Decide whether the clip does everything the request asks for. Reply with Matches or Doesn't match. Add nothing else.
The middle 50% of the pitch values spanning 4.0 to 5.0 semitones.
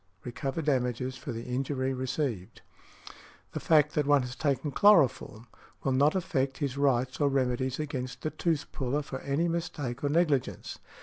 Doesn't match